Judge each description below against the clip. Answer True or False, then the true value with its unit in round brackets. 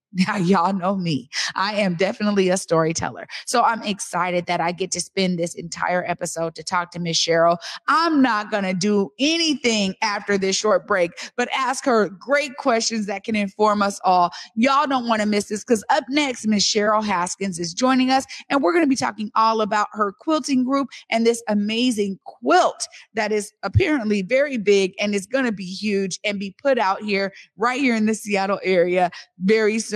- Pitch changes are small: False (3.5 semitones)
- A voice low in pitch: False (205 Hz)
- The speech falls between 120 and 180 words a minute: False (200 wpm)